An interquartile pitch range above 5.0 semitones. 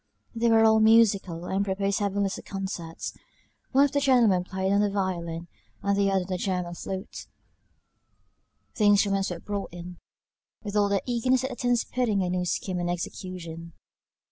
No: average, 3.3 semitones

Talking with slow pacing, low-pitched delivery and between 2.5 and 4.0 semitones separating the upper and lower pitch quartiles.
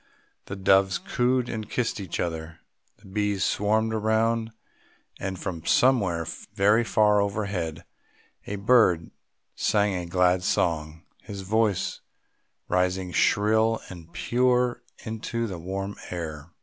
Yes: slow, 120 wpm; low, 100 Hz; average, 3.6 semitones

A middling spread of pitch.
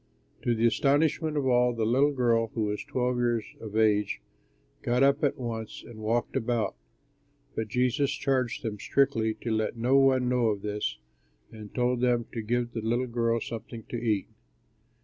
No: narrow, 2.2 semitones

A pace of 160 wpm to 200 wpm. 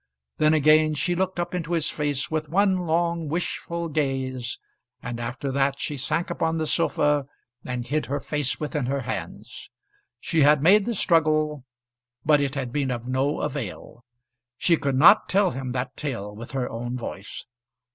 Yes: average, 170 wpm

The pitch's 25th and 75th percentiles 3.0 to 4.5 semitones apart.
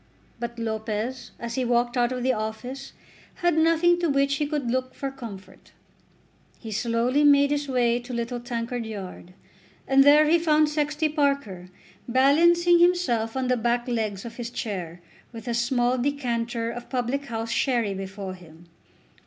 Yes: average, 3.6 semitones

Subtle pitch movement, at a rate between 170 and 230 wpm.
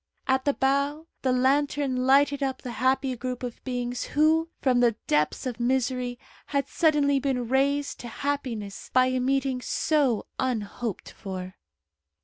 No: narrow, 2.3 semitones; average, 145 wpm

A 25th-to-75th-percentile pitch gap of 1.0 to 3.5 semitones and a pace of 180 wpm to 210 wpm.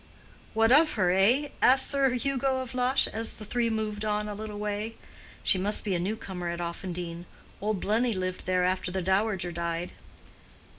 No: average, 3.9 semitones; average, 185 wpm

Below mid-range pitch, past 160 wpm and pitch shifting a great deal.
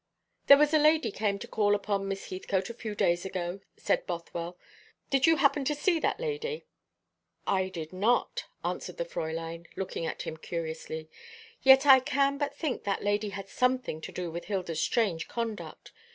No: high, 205 Hz; average, 180 wpm; wide, 7.8 semitones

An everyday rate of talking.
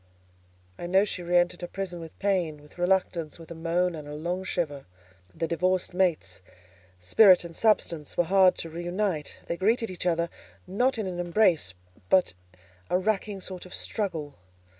Yes: average, 175 wpm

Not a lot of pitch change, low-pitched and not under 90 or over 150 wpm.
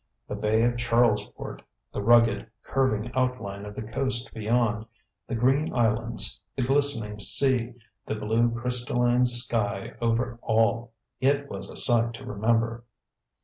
Yes: narrow, 1.8 semitones; low, 115 Hz; slow, 135 wpm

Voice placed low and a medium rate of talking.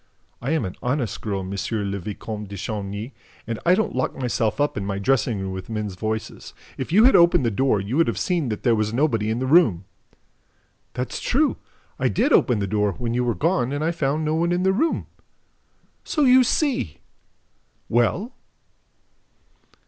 Yes: low, 120 Hz; average, 190 wpm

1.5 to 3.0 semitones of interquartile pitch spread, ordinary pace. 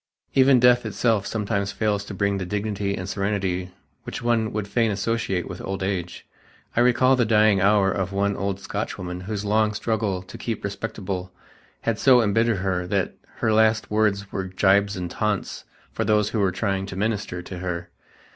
Yes: narrow, 2.4 semitones; average, 180 wpm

